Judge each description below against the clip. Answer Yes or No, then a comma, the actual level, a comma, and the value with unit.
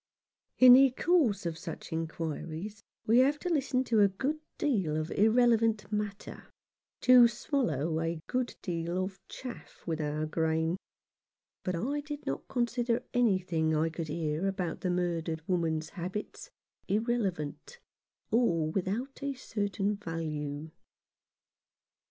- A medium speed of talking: No, slow, 130 wpm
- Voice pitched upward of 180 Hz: Yes, high, 190 Hz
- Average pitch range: No, wide, 6.7 semitones